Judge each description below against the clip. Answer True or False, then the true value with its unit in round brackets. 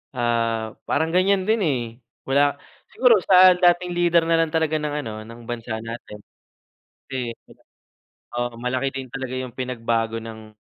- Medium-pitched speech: False (130 Hz)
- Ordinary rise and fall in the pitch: False (6.1 semitones)